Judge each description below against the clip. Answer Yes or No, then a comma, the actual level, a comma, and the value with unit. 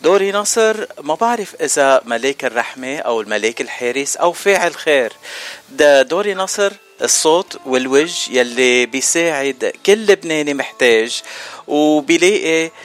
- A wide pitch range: Yes, wide, 7.2 semitones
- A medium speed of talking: Yes, average, 110 wpm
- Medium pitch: Yes, medium, 155 Hz